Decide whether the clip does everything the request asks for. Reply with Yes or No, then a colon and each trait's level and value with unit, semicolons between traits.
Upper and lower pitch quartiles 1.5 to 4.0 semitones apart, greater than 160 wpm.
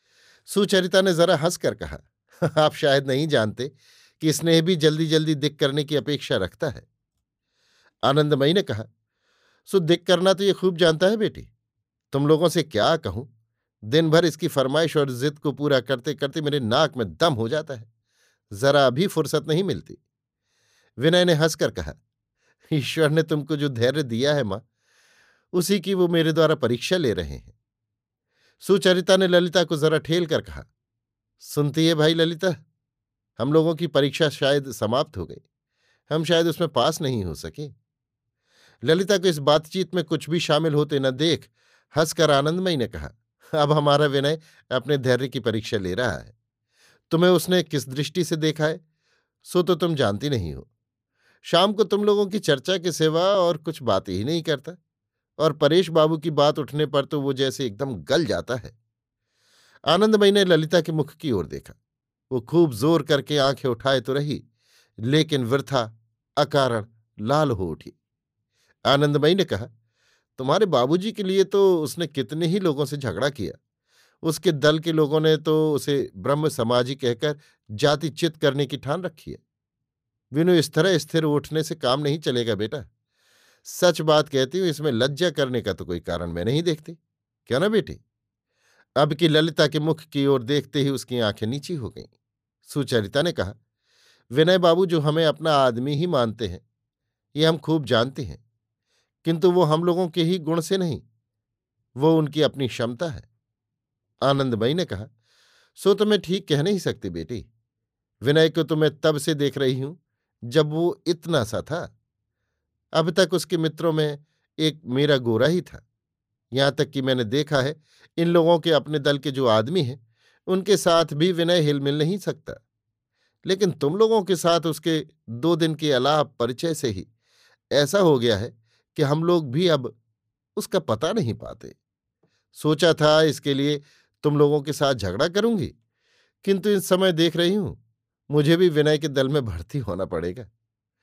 No: average, 5.3 semitones; average, 175 wpm